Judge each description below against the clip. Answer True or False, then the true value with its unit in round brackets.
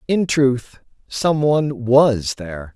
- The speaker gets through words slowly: True (130 wpm)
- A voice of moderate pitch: False (130 Hz)